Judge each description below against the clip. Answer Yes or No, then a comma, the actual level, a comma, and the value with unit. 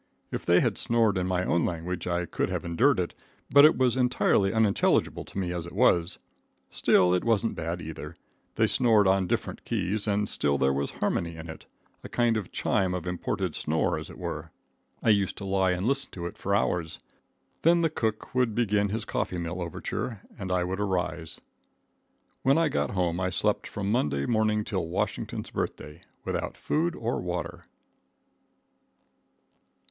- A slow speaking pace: No, average, 180 wpm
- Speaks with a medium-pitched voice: No, very low, 95 Hz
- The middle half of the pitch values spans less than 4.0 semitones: No, average, 4.3 semitones